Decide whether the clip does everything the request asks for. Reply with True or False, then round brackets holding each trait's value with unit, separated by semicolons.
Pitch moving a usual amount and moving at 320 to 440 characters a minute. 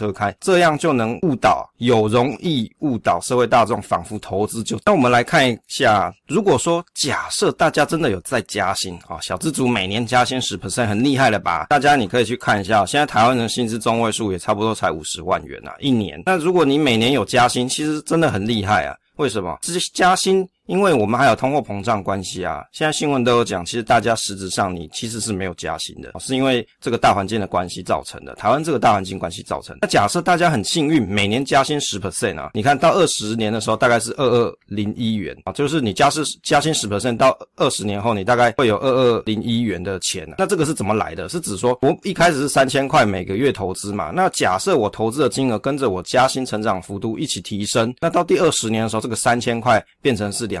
True (4.9 semitones; 375 characters per minute)